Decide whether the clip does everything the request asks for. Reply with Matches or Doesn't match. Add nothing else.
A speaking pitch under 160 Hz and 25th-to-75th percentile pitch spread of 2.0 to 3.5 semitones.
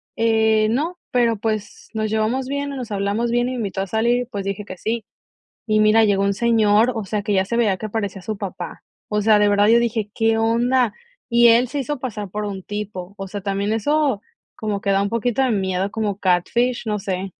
Doesn't match